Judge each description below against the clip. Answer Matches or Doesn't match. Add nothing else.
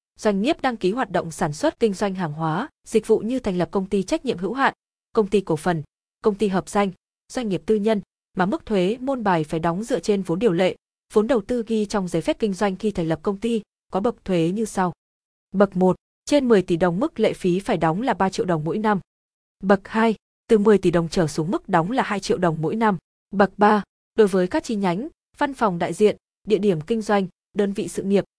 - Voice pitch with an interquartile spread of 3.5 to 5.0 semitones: Matches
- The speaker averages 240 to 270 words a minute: Matches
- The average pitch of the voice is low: Doesn't match